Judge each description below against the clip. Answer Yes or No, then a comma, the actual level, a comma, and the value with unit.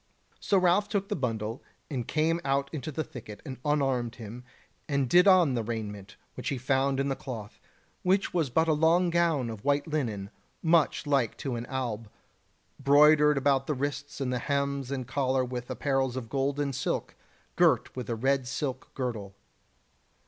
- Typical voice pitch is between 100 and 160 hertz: Yes, low, 135 Hz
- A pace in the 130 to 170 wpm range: No, average, 180 wpm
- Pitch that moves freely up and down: No, average, 3.3 semitones